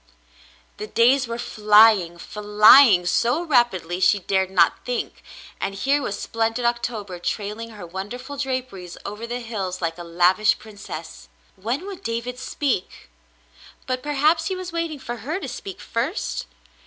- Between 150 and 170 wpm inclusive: Yes, average, 155 wpm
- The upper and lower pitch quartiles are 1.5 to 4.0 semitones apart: No, average, 5.1 semitones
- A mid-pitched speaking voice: No, high, 230 Hz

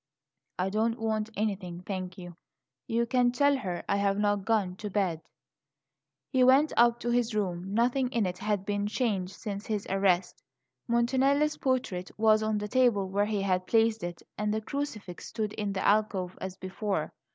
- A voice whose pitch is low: No, high, 210 Hz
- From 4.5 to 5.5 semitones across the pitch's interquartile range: No, average, 3.4 semitones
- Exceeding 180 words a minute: No, average, 175 wpm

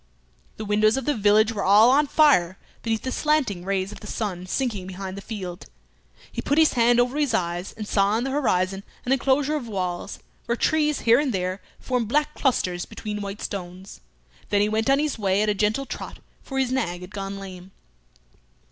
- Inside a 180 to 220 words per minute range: Yes, average, 200 wpm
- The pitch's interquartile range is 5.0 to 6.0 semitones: Yes, average, 5.3 semitones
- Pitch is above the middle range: Yes, high, 215 Hz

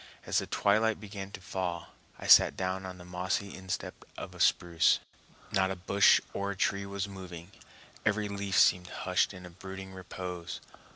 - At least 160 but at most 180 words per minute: Yes, average, 165 wpm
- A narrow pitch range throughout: Yes, narrow, 1.6 semitones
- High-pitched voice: No, very low, 95 Hz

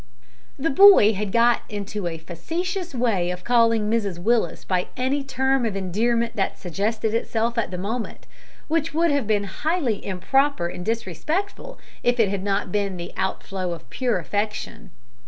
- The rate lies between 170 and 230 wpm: No, average, 160 wpm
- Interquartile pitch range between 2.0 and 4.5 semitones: No, average, 5.0 semitones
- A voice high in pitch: Yes, high, 220 Hz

